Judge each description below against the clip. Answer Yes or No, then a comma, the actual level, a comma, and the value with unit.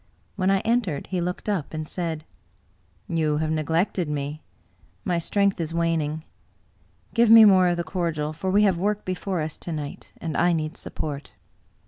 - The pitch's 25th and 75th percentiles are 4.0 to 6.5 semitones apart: No, average, 3.5 semitones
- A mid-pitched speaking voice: Yes, medium, 170 Hz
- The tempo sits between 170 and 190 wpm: Yes, average, 175 wpm